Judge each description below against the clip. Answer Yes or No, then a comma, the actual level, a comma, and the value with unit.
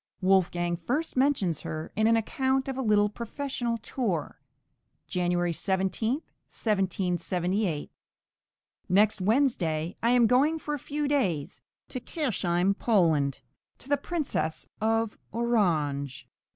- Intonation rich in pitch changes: Yes, wide, 6.2 semitones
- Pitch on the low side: No, high, 210 Hz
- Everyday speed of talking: No, slow, 120 wpm